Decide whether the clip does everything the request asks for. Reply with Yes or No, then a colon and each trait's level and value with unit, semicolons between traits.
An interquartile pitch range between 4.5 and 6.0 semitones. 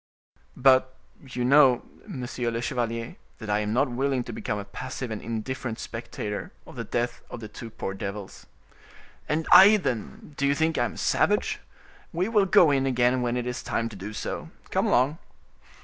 No: average, 3.1 semitones